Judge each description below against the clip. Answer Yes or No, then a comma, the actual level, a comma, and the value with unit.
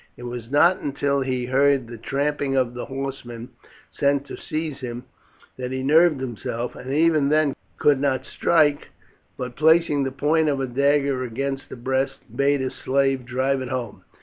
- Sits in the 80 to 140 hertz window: Yes, low, 135 Hz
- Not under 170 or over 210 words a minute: Yes, average, 175 wpm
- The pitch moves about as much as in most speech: No, narrow, 2.0 semitones